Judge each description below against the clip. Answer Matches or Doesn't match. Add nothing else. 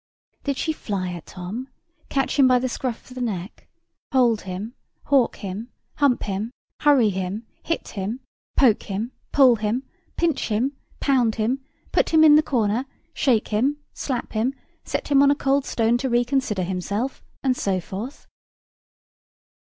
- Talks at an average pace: Matches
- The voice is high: Matches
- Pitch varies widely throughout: Doesn't match